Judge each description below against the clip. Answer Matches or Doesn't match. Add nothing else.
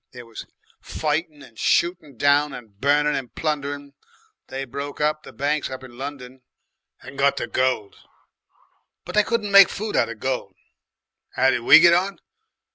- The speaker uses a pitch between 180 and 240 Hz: Doesn't match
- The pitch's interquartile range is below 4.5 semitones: Matches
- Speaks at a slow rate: Doesn't match